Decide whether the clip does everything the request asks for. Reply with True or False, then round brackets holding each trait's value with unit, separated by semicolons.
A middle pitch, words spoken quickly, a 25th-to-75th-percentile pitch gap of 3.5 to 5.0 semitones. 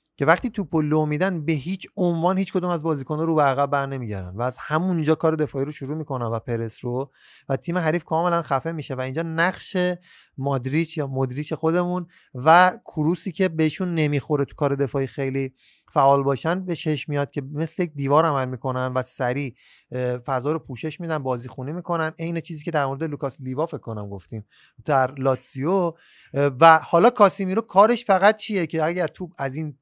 True (155 Hz; 185 wpm; 3.9 semitones)